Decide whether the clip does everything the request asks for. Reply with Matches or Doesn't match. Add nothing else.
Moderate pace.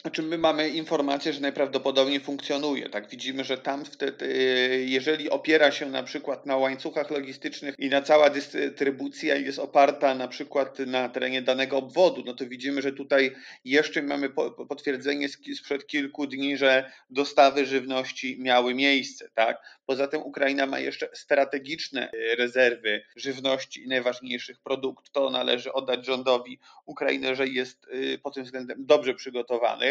Matches